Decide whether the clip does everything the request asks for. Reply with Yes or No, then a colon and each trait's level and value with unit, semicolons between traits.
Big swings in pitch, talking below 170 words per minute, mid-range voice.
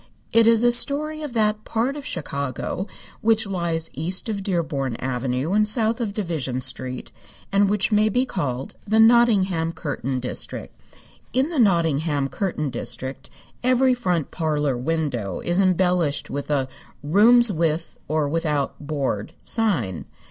Yes: wide, 7.4 semitones; average, 140 wpm; medium, 170 Hz